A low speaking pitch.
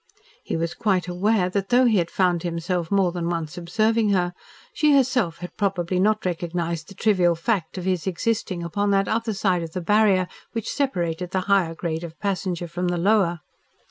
No: medium, 180 Hz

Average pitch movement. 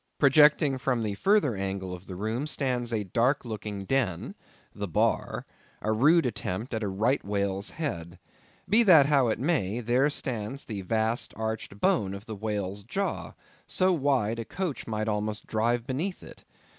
Yes: average, 5.0 semitones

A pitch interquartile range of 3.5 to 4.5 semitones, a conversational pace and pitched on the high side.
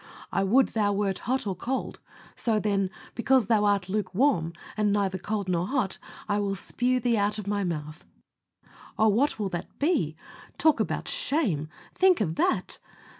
Yes: average, 4.0 semitones; average, 170 wpm; high, 205 Hz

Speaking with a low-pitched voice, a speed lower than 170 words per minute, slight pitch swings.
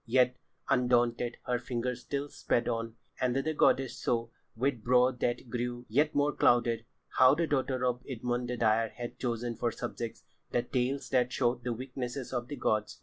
No: low, 125 Hz; average, 175 wpm; narrow, 1.4 semitones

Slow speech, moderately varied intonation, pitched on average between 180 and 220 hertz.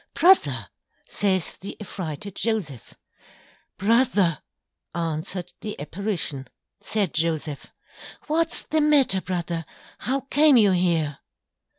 No: slow, 95 wpm; wide, 5.8 semitones; high, 190 Hz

